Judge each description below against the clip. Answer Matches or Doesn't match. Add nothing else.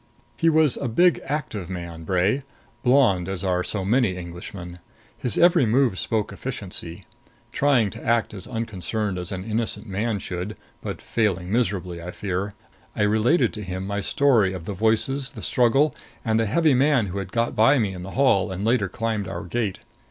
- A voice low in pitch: Matches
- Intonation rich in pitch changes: Doesn't match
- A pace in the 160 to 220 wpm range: Matches